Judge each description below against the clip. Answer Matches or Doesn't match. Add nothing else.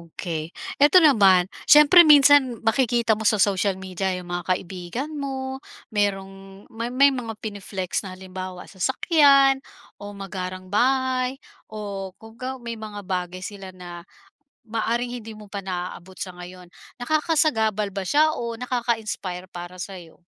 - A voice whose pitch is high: Matches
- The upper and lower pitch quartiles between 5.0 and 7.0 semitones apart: Matches